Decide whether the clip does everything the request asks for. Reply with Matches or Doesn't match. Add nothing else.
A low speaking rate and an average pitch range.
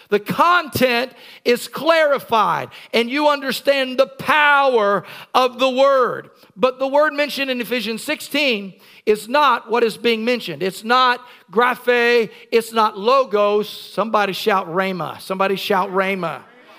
Matches